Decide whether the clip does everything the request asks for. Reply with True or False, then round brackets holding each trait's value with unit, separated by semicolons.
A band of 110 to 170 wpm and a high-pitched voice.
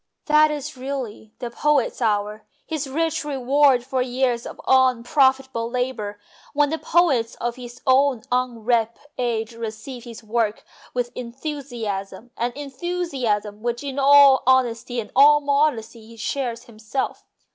True (135 wpm; 250 Hz)